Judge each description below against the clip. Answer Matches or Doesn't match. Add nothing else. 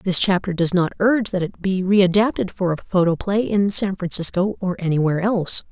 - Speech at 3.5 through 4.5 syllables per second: Doesn't match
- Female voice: Matches